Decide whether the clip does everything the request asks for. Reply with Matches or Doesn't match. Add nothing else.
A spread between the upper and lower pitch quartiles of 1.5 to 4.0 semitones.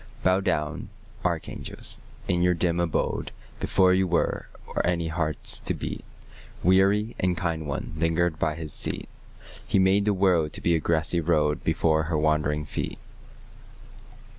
Matches